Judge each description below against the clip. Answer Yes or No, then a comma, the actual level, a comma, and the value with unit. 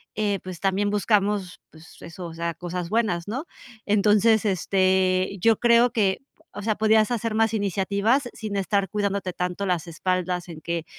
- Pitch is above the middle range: Yes, high, 200 Hz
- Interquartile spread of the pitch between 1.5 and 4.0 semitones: Yes, average, 2.9 semitones